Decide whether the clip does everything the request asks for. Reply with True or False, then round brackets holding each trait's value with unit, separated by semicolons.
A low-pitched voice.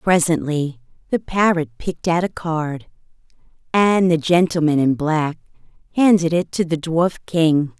False (165 Hz)